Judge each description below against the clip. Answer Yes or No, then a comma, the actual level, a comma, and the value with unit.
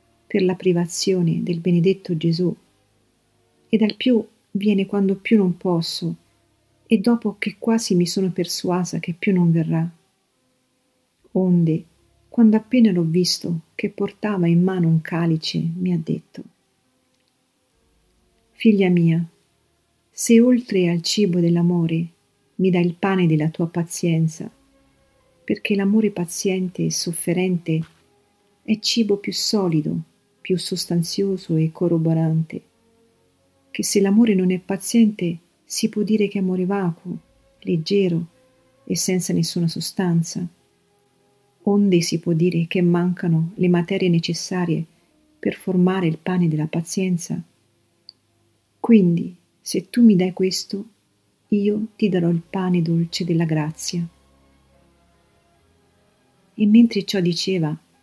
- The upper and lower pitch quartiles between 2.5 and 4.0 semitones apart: Yes, average, 3.1 semitones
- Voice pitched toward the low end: No, medium, 175 Hz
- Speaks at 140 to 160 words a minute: No, average, 120 wpm